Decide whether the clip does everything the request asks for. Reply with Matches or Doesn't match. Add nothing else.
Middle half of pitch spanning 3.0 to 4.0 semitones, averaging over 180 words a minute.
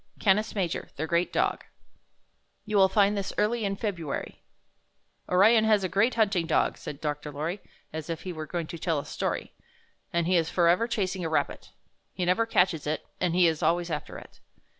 Matches